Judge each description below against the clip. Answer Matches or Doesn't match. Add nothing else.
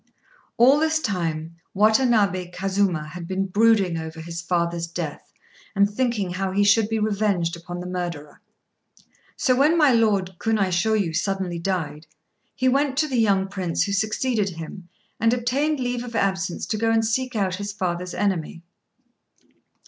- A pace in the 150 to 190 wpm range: Matches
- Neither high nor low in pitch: Doesn't match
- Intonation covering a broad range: Doesn't match